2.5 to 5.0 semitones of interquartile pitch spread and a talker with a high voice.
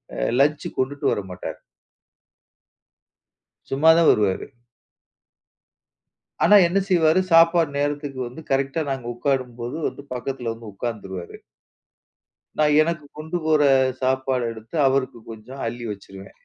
No: average, 4.6 semitones; low, 135 Hz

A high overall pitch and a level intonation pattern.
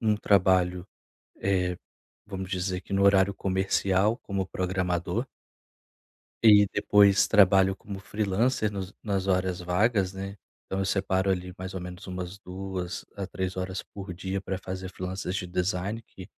No: very low, 95 Hz; narrow, 1.3 semitones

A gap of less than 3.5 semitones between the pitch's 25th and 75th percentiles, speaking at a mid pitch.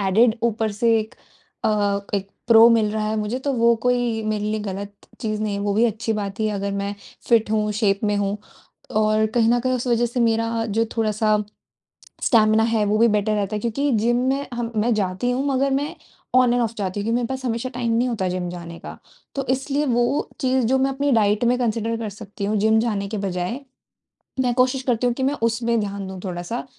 No: narrow, 2.6 semitones; high, 225 Hz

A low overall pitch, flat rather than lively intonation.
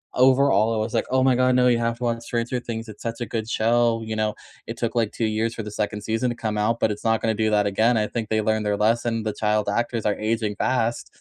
Yes: low, 115 Hz; narrow, 1.6 semitones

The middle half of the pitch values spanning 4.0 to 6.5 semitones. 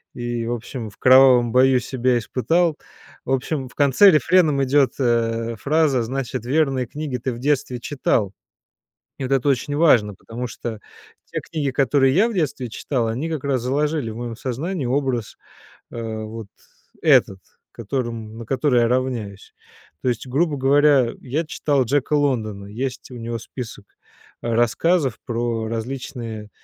No: average, 3.4 semitones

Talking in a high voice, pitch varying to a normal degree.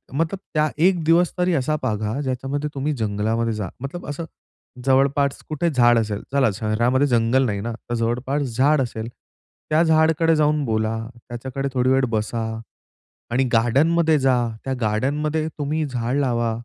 No: low, 135 Hz; average, 4.6 semitones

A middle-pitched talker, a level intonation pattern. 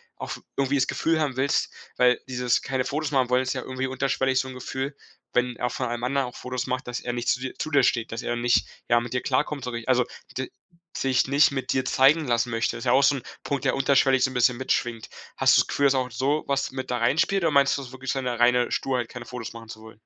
No: low, 130 Hz; narrow, 1.8 semitones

